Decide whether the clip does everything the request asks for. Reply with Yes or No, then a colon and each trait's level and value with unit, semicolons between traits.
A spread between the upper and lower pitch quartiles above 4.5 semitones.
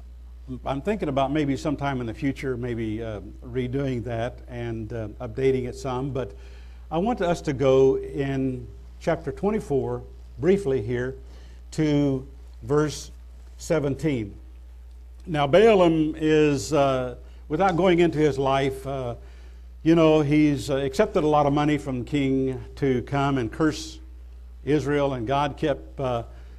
Yes: wide, 5.6 semitones